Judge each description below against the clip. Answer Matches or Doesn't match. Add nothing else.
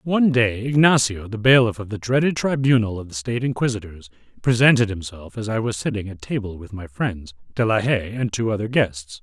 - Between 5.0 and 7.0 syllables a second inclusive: Matches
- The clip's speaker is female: Doesn't match